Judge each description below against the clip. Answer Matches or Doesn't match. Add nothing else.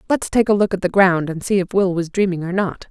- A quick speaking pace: Matches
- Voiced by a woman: Matches